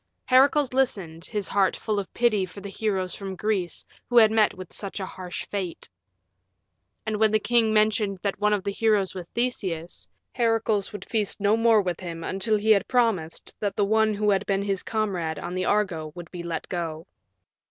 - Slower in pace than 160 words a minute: No, average, 195 wpm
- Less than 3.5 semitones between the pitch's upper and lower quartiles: Yes, average, 2.9 semitones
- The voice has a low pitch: No, high, 200 Hz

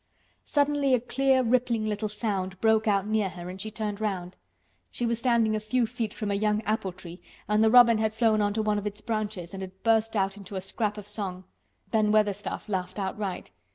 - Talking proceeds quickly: Yes, fast, 220 wpm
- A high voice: Yes, high, 215 Hz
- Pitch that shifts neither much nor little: No, narrow, 2.1 semitones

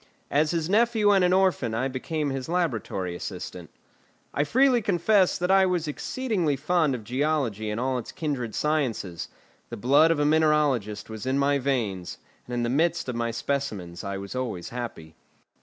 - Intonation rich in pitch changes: Yes, wide, 6.1 semitones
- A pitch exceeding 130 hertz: Yes, medium, 140 Hz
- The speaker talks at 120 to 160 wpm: No, average, 175 wpm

